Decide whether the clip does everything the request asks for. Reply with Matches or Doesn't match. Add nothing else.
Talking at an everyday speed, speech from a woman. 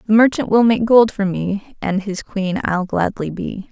Doesn't match